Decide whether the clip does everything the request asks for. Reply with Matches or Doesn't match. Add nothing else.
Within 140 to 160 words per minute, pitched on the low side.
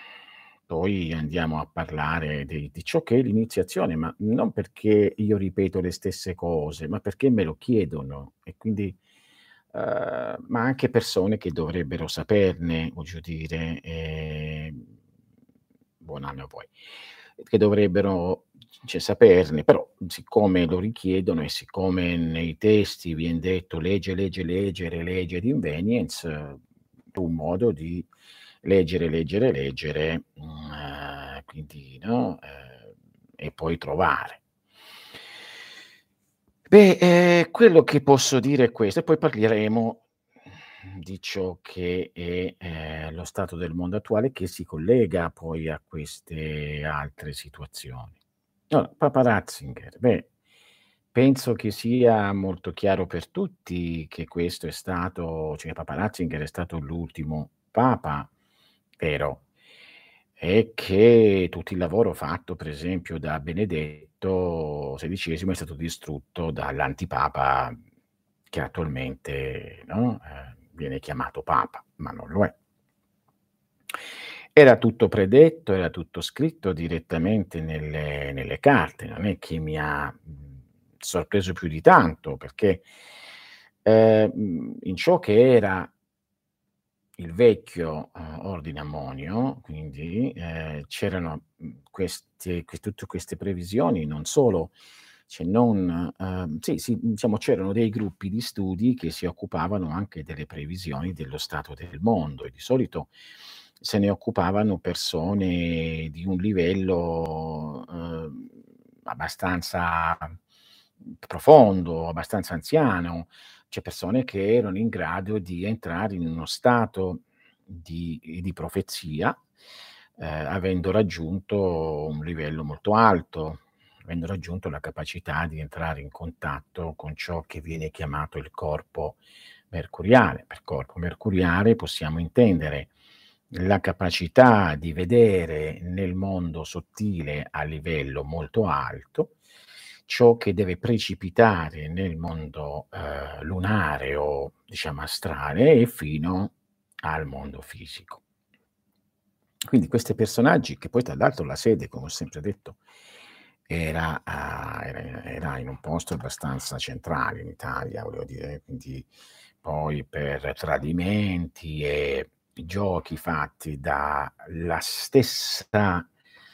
Doesn't match